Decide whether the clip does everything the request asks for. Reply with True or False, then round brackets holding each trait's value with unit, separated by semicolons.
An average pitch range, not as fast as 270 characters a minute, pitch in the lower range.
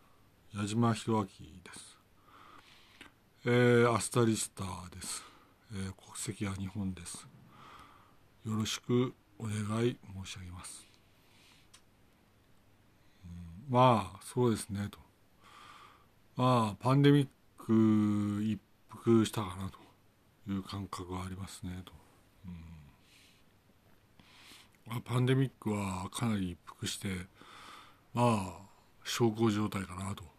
True (3.0 semitones; 200 characters per minute; 105 Hz)